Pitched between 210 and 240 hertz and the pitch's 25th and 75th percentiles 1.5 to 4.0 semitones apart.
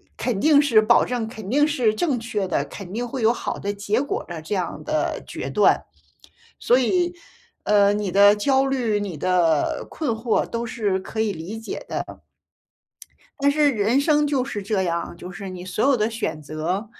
No: high, 215 Hz; average, 4.8 semitones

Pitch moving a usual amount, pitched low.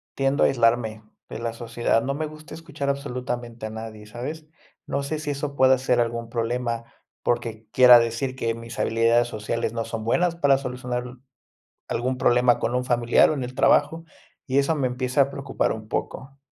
Yes: average, 3.0 semitones; low, 125 Hz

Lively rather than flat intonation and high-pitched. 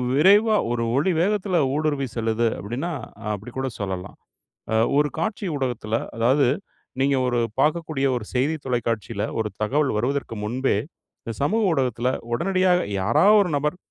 No: wide, 5.7 semitones; low, 135 Hz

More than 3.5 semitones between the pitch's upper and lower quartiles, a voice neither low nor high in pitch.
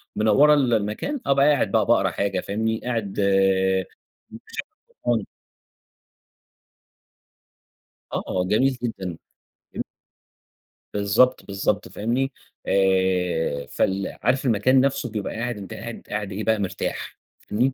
No: average, 4.1 semitones; low, 105 Hz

